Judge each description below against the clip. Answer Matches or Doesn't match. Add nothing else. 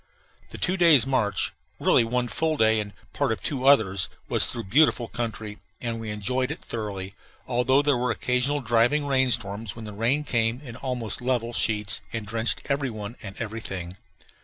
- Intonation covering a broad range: Doesn't match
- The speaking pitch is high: Doesn't match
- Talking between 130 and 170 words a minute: Doesn't match